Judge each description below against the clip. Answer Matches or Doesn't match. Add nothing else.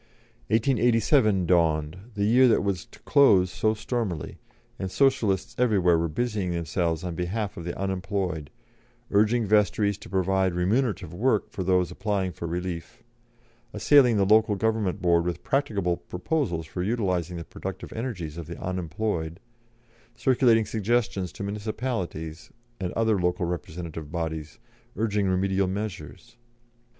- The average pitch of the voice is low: Matches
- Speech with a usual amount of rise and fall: Matches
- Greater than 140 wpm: Doesn't match